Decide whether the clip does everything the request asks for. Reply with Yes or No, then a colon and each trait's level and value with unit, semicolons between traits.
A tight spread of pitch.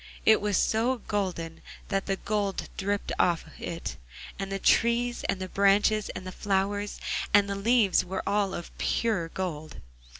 Yes: narrow, 1.9 semitones